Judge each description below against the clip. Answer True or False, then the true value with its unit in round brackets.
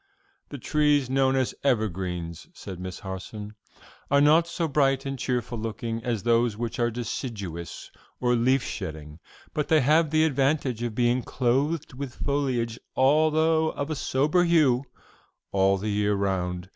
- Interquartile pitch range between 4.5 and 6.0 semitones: True (5.2 semitones)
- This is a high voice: False (125 Hz)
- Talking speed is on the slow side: False (150 wpm)